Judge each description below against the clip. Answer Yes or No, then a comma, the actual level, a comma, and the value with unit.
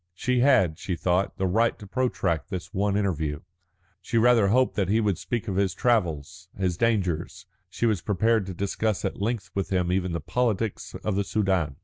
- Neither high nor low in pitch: No, low, 100 Hz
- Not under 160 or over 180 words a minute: No, average, 195 wpm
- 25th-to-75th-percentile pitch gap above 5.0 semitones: No, average, 3.8 semitones